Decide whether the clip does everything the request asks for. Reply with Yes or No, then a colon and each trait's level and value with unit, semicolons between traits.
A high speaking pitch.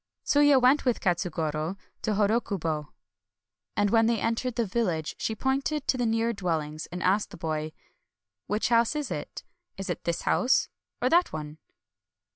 Yes: high, 210 Hz